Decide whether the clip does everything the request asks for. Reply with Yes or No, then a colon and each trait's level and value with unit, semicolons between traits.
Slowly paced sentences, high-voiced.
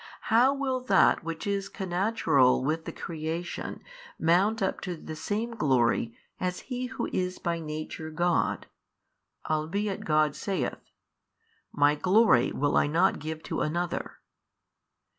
No: slow, 130 wpm; medium, 175 Hz